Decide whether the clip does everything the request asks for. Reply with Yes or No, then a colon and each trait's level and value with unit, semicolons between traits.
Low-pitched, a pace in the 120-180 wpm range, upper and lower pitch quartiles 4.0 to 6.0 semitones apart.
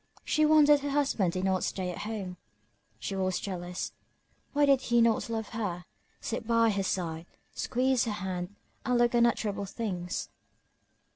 No: high, 215 Hz; average, 155 wpm; average, 4.6 semitones